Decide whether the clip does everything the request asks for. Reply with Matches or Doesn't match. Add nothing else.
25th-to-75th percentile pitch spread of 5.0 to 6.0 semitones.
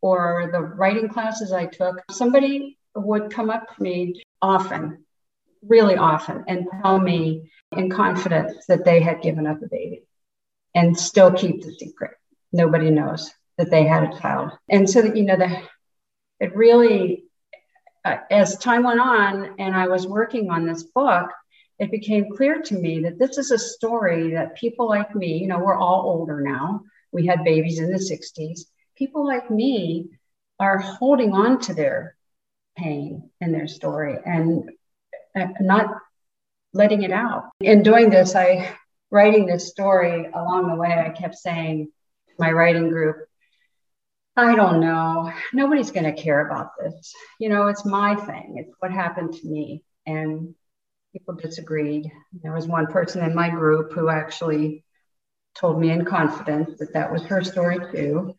Doesn't match